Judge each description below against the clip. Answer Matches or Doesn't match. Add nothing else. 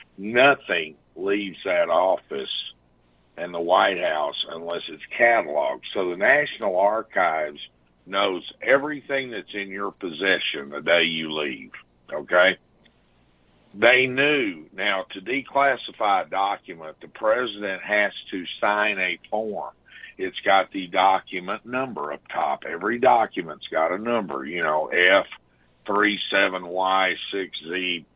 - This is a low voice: Matches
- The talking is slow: Matches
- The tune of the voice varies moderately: Doesn't match